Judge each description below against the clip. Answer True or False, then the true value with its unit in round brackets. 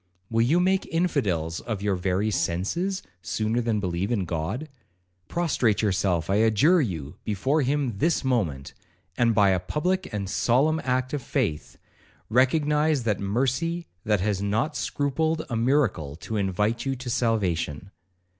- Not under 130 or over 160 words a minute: True (145 wpm)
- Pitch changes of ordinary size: False (6.7 semitones)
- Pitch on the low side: True (115 Hz)